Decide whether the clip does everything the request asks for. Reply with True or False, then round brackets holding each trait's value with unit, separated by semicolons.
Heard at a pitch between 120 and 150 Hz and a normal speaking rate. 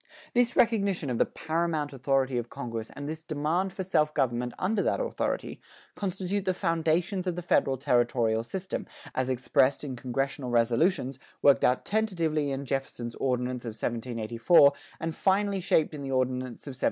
True (140 Hz; 165 wpm)